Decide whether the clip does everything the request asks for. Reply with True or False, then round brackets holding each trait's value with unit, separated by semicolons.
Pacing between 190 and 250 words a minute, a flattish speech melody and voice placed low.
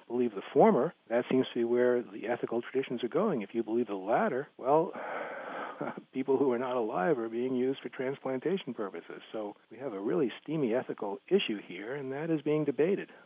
True (200 wpm; 2.1 semitones; 125 Hz)